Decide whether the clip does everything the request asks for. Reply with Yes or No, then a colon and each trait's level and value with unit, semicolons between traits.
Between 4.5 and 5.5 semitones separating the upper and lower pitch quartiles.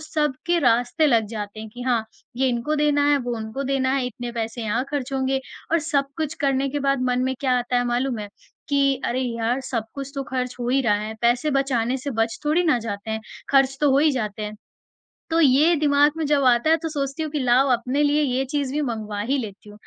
No: average, 3.1 semitones